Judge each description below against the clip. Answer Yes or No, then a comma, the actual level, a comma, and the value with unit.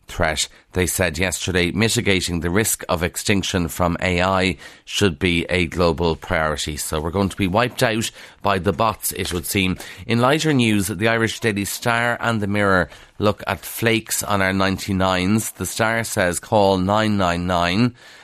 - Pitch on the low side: Yes, very low, 95 Hz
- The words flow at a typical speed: Yes, average, 165 wpm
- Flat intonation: No, average, 3.8 semitones